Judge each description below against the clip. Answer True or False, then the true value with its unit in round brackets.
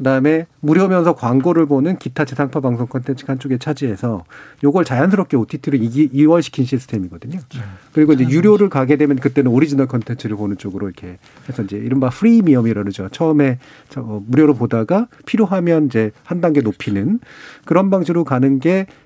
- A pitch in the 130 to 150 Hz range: True (140 Hz)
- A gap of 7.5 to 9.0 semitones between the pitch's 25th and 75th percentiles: False (5.2 semitones)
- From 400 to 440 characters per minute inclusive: True (410 characters per minute)